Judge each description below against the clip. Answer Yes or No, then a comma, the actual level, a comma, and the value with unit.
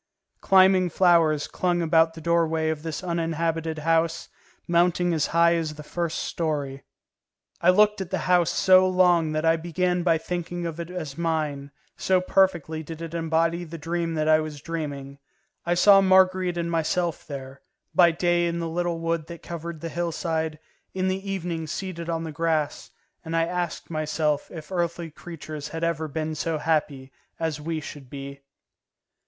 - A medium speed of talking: Yes, average, 170 wpm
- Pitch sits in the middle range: Yes, medium, 165 Hz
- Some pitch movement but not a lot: No, narrow, 1.8 semitones